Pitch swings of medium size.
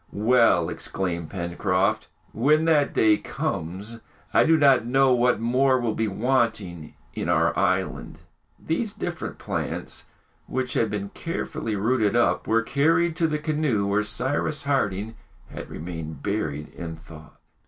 No: wide, 6.3 semitones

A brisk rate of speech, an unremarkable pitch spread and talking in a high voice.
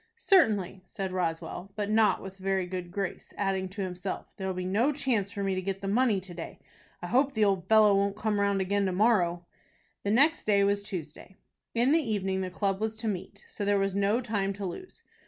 No: fast, 220 wpm; narrow, 2.3 semitones; high, 200 Hz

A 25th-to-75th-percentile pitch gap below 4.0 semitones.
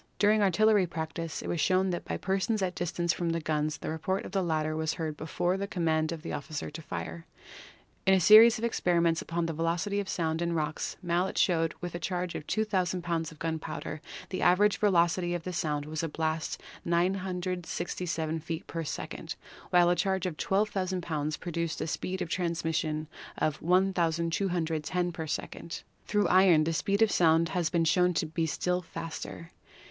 Yes: narrow, 2.4 semitones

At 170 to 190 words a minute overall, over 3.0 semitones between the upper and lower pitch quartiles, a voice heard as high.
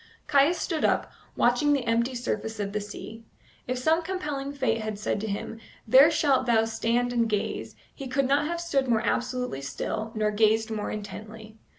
Yes: average, 185 wpm; average, 4.1 semitones; high, 235 Hz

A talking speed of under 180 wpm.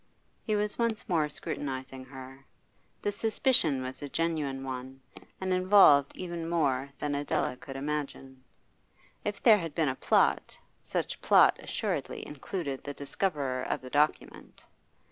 Yes: average, 140 wpm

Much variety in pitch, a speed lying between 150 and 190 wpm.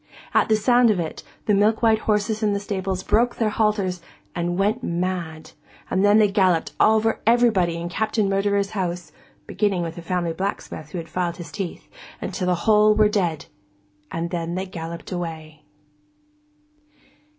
No: average, 3.7 semitones; average, 170 wpm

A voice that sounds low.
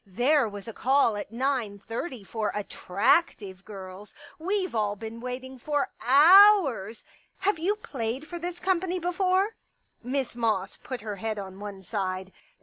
No: high, 240 Hz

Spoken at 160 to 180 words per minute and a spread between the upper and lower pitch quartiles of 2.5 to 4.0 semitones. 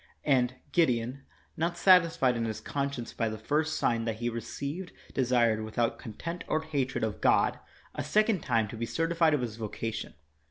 No: average, 175 wpm; wide, 5.6 semitones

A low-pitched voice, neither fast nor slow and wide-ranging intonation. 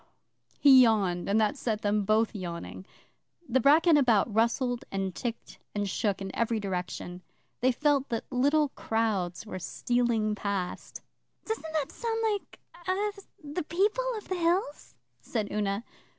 No: high, 230 Hz; average, 145 wpm; wide, 6.4 semitones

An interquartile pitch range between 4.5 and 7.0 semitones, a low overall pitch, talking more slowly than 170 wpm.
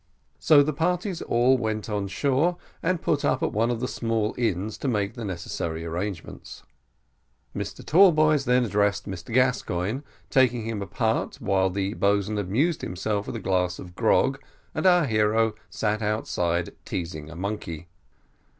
Yes: average, 5.3 semitones; low, 110 Hz; average, 155 wpm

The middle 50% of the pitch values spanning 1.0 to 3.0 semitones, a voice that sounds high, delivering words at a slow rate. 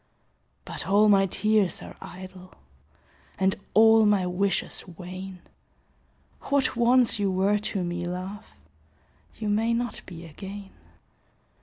Yes: average, 2.7 semitones; high, 195 Hz; slow, 120 wpm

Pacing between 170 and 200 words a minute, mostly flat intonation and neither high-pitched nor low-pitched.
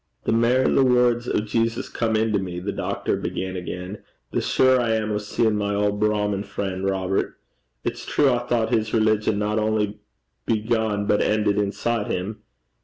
No: average, 175 wpm; narrow, 2.0 semitones; low, 105 Hz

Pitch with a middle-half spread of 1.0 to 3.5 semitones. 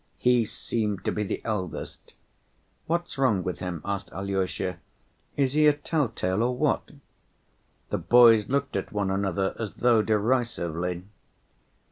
No: average, 4.5 semitones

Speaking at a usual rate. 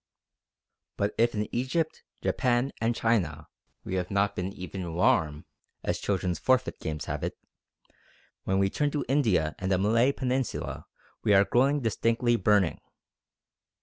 Yes: average, 145 wpm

